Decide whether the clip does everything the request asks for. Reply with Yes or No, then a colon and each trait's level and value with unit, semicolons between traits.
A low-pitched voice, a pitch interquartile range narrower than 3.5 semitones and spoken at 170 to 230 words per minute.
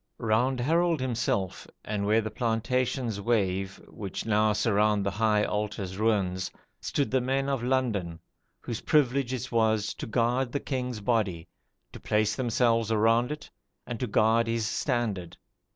No: low, 115 Hz; average, 3.1 semitones; average, 150 wpm